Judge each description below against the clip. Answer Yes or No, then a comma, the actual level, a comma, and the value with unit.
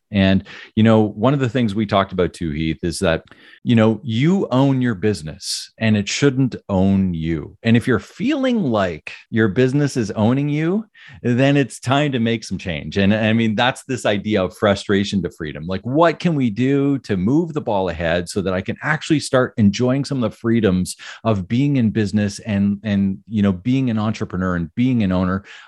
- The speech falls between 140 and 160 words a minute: No, fast, 205 wpm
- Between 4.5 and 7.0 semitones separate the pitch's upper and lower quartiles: Yes, average, 4.8 semitones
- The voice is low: Yes, low, 110 Hz